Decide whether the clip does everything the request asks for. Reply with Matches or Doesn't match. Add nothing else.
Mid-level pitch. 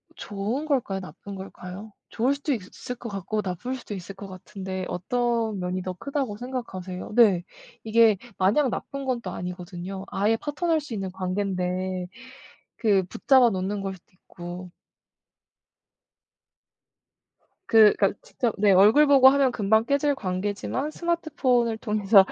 Doesn't match